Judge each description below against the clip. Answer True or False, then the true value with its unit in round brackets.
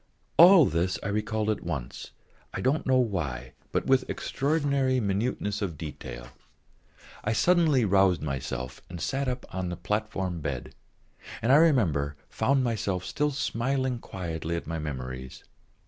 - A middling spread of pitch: False (8.1 semitones)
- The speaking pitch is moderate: False (100 Hz)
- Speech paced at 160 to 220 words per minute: False (145 wpm)